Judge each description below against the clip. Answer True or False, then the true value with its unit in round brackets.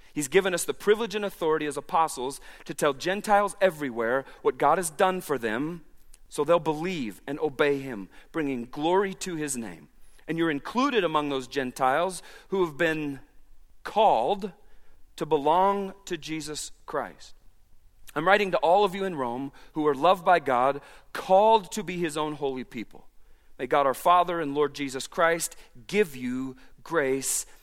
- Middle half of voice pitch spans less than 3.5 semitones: False (5.3 semitones)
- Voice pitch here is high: False (155 Hz)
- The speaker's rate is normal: True (165 wpm)